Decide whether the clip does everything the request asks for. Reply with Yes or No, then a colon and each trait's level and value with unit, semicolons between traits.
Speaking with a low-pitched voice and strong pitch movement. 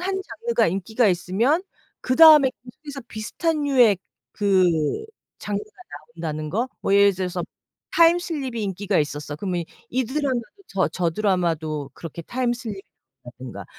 No: high, 210 Hz; wide, 7.0 semitones